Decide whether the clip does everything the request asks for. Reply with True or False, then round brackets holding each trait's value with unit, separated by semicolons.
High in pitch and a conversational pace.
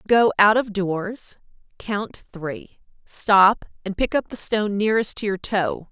True (205 Hz; 160 wpm)